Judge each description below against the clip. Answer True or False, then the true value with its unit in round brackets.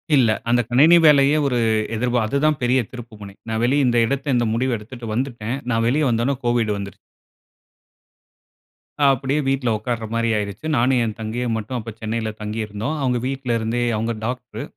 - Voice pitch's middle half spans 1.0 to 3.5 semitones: True (2.9 semitones)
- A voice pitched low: True (120 Hz)